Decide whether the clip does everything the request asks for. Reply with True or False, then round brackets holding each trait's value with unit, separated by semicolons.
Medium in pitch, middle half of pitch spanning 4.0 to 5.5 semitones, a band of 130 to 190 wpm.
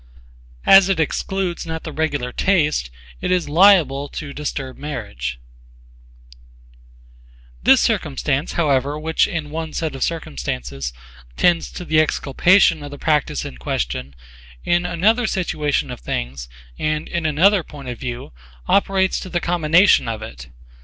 True (155 Hz; 5.0 semitones; 140 wpm)